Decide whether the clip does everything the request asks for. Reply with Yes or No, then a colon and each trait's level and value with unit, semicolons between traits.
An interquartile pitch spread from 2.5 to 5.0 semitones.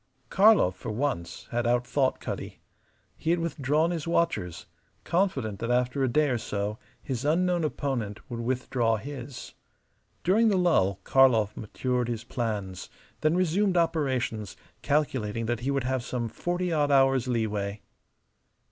No: wide, 5.4 semitones